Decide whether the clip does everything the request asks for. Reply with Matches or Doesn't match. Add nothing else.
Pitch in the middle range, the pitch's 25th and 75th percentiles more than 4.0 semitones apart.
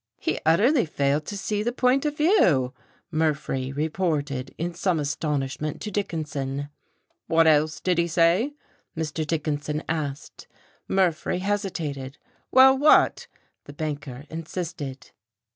Matches